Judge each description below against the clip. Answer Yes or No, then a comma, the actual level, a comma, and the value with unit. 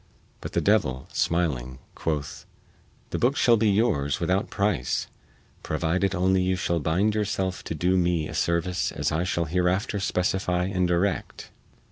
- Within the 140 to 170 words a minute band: Yes, average, 150 wpm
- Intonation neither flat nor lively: Yes, average, 3.0 semitones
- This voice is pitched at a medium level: No, very low, 90 Hz